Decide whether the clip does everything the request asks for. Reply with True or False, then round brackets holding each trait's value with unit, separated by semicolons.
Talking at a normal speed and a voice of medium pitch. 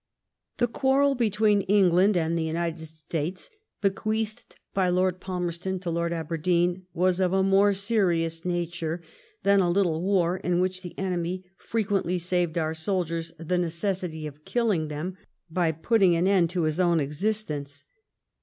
True (150 wpm; 180 Hz)